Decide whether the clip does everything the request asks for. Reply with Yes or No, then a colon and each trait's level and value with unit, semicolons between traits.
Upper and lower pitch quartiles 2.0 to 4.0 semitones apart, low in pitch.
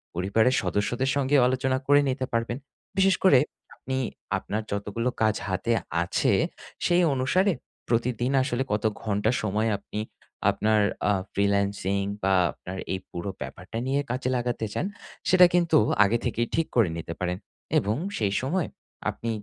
No: average, 4.6 semitones; low, 115 Hz